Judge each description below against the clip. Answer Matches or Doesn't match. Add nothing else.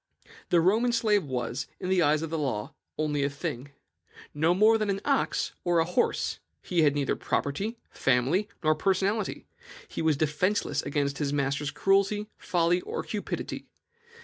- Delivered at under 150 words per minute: Doesn't match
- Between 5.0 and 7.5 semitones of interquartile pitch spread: Matches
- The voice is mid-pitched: Matches